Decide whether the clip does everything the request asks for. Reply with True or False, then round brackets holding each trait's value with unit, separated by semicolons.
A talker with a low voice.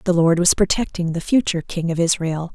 False (175 Hz)